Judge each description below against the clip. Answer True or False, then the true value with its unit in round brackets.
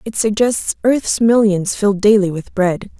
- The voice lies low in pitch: False (205 Hz)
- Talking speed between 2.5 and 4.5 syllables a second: True (4.4 syllables/s)